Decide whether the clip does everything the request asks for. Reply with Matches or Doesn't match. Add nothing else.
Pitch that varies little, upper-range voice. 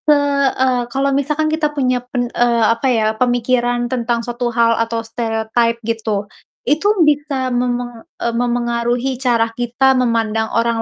Matches